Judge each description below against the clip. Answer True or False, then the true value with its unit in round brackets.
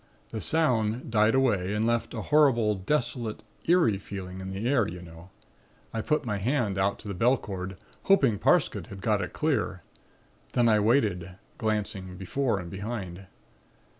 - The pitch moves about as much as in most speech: True (4.0 semitones)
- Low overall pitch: True (105 Hz)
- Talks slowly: False (165 wpm)